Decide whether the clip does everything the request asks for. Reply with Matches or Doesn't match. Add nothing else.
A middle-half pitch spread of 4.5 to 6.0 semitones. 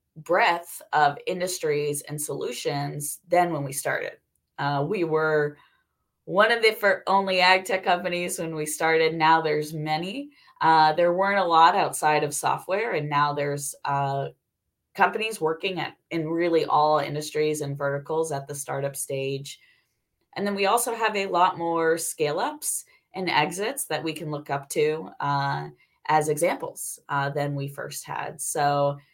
Doesn't match